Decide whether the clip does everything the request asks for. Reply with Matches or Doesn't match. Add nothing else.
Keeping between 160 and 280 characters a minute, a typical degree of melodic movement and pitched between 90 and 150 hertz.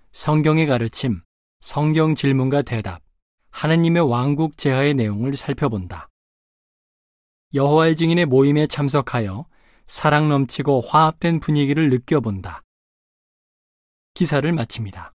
Matches